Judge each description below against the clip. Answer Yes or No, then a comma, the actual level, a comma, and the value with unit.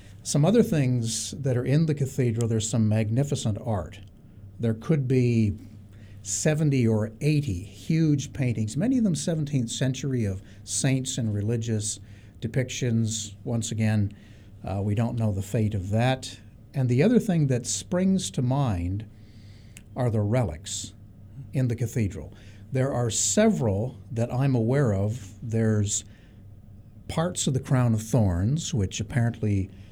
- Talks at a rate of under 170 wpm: Yes, average, 140 wpm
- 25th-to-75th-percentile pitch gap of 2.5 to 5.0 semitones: Yes, average, 4.2 semitones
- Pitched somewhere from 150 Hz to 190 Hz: No, low, 115 Hz